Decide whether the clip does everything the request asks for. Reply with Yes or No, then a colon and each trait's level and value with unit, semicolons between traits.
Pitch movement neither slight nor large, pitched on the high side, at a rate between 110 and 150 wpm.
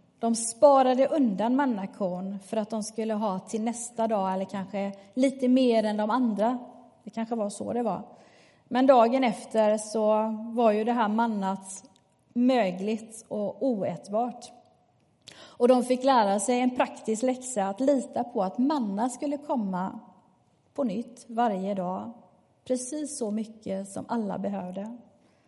Yes: average, 3.4 semitones; high, 225 Hz; average, 145 wpm